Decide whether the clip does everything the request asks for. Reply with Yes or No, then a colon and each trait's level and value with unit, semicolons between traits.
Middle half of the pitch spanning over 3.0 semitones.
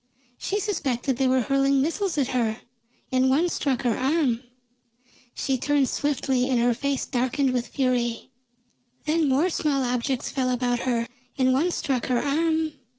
No: average, 2.7 semitones